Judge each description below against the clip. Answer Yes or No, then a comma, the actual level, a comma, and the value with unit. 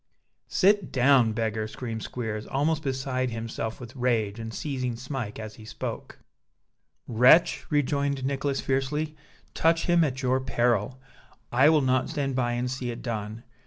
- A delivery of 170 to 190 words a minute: No, average, 150 wpm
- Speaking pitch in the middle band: No, low, 130 Hz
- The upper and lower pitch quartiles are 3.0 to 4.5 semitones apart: Yes, average, 3.4 semitones